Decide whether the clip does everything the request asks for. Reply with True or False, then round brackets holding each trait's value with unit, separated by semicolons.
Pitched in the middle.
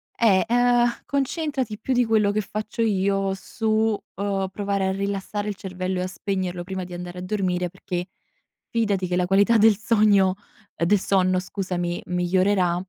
False (195 Hz)